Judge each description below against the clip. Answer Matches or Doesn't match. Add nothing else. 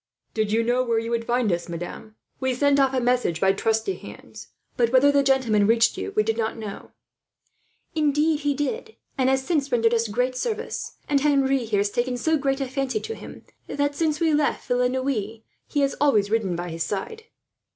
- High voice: Matches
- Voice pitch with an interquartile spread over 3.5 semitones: Matches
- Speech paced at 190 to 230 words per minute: Matches